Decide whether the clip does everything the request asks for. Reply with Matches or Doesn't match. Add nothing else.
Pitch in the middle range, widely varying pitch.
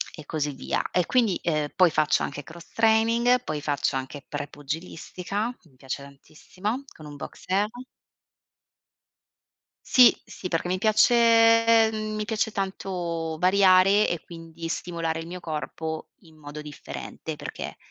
Matches